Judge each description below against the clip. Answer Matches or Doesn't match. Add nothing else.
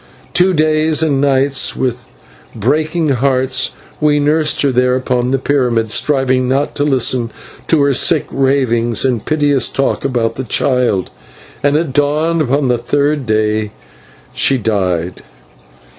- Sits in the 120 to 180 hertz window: Matches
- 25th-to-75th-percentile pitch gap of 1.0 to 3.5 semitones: Matches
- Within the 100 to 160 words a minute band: Matches